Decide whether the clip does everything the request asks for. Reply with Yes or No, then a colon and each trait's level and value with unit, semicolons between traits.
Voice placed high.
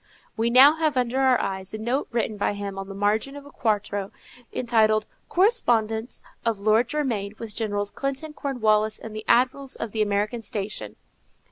Yes: high, 220 Hz